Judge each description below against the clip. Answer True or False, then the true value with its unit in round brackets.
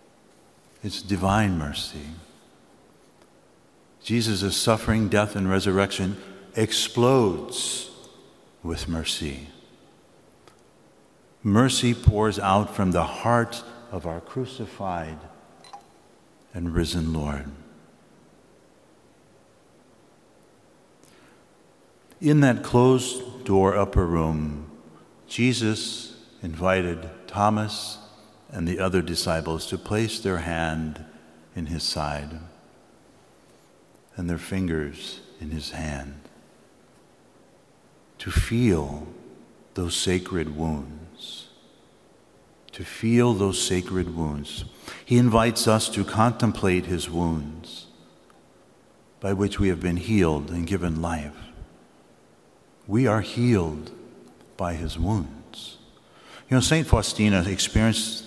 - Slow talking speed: True (90 wpm)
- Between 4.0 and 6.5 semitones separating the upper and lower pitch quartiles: True (5.2 semitones)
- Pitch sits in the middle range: False (95 Hz)